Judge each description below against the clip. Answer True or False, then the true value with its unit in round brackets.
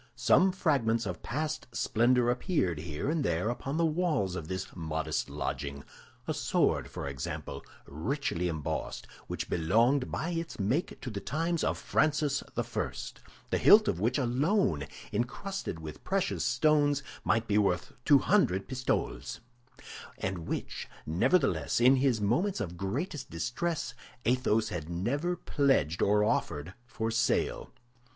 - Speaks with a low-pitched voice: True (120 Hz)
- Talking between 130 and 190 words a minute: True (140 wpm)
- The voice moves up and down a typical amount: False (8.6 semitones)